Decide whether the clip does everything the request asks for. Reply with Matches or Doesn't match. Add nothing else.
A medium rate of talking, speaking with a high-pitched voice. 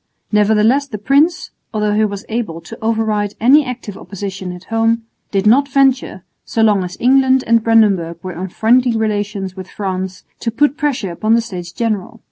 Matches